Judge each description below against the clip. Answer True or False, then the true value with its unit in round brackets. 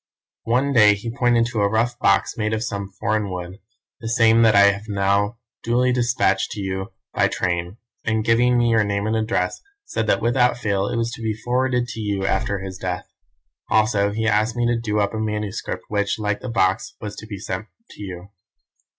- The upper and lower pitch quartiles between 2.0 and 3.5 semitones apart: True (2.6 semitones)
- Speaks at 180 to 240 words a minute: True (205 wpm)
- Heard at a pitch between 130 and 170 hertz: False (110 Hz)